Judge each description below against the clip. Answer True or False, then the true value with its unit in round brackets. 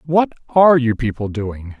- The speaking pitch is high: False (125 Hz)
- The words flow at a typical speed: True (165 wpm)